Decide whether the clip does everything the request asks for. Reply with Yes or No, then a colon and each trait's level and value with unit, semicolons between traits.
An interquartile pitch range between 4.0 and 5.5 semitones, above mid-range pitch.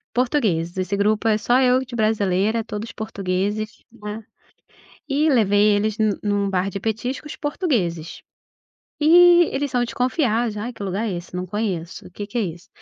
No: average, 3.4 semitones; high, 215 Hz